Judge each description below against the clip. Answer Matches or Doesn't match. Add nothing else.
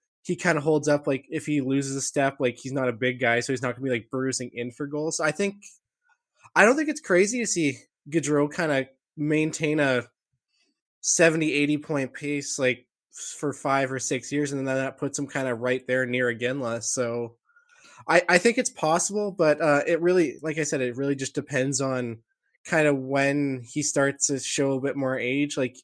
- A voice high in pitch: Doesn't match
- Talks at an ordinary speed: Doesn't match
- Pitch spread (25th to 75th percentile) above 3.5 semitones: Doesn't match